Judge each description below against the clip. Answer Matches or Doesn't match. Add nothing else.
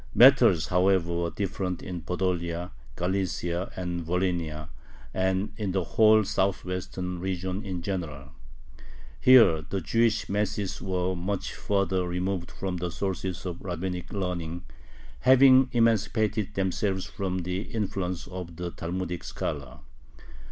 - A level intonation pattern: Matches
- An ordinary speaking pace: Doesn't match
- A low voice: Matches